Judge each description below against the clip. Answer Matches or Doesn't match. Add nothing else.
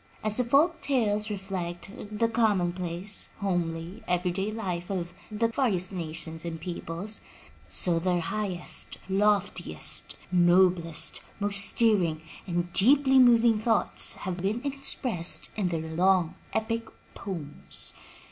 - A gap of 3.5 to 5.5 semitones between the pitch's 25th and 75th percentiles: Matches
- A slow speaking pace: Matches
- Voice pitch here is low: Doesn't match